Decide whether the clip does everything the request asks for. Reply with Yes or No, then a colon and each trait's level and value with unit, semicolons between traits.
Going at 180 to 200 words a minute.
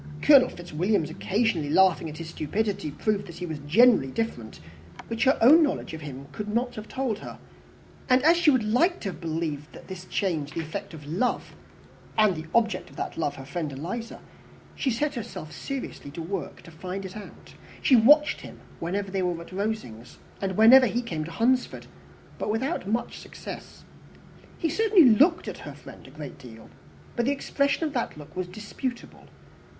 Yes: average, 185 wpm